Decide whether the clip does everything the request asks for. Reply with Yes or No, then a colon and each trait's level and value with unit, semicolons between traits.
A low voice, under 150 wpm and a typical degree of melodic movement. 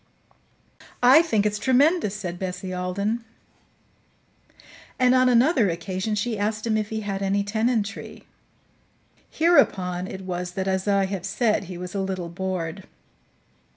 No: high, 200 Hz; average, 140 wpm; average, 3.1 semitones